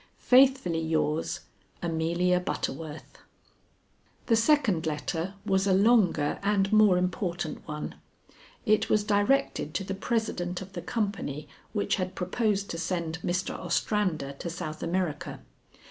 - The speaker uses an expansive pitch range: No, average, 4.1 semitones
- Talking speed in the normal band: No, slow, 125 wpm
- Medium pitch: Yes, medium, 180 Hz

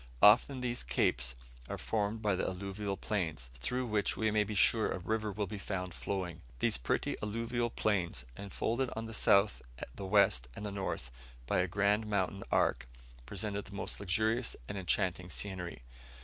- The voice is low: Yes, low, 100 Hz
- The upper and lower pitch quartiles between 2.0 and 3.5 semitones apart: Yes, average, 2.9 semitones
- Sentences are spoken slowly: No, average, 165 wpm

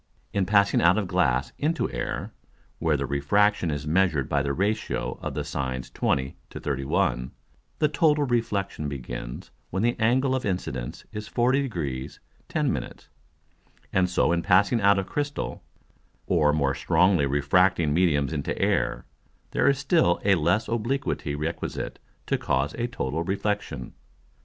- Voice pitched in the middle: No, very low, 90 Hz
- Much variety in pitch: Yes, wide, 7.1 semitones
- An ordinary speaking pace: Yes, average, 150 wpm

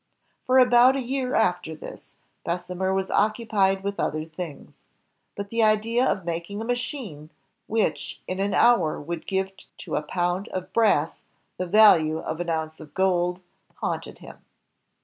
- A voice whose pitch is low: No, high, 190 Hz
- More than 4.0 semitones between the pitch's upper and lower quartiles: Yes, average, 4.7 semitones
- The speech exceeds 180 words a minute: No, average, 155 wpm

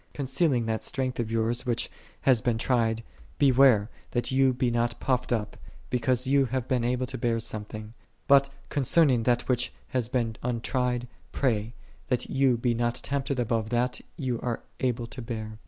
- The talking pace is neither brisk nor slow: Yes, average, 170 wpm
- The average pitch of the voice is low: Yes, low, 125 Hz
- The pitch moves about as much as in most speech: No, narrow, 2.1 semitones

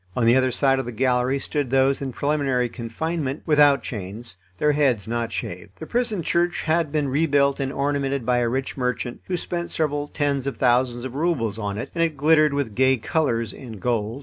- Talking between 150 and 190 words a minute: No, fast, 205 wpm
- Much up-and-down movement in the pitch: No, average, 3.4 semitones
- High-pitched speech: No, low, 135 Hz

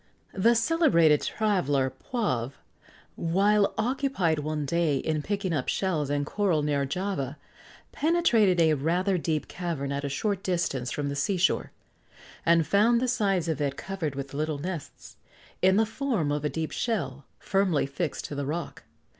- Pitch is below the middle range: No, medium, 170 Hz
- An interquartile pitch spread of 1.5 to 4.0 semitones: No, wide, 5.6 semitones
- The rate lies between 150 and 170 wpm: Yes, average, 160 wpm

